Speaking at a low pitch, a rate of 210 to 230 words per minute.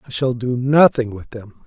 Yes: low, 125 Hz; fast, 215 wpm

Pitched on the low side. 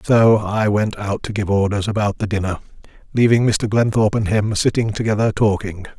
Yes: low, 105 Hz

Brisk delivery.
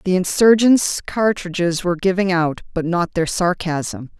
No: average, 145 wpm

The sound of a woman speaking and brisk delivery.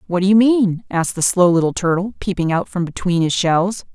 Yes: female; fast, 230 wpm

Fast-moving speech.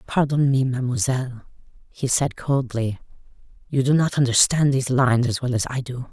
No: average, 165 wpm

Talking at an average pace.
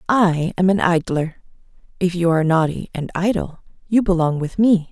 Yes: average, 170 wpm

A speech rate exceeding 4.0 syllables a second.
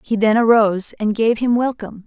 Yes: 5.7 syllables/s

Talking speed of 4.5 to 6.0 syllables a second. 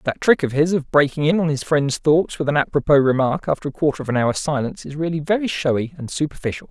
No: 6.4 syllables/s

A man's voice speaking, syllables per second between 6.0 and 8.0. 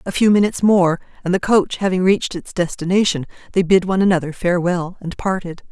No: female; 6.2 syllables/s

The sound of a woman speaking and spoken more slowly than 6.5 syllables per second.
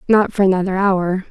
Yes: female; 5.4 syllables/s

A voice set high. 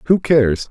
No: low, 130 Hz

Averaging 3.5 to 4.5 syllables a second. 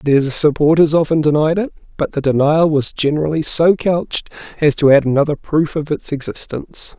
No: 5.4 syllables/s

